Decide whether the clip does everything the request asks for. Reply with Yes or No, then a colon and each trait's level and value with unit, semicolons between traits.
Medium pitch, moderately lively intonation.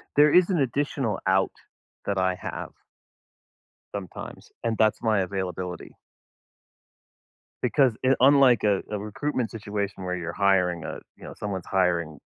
No: low, 100 Hz; average, 4.6 semitones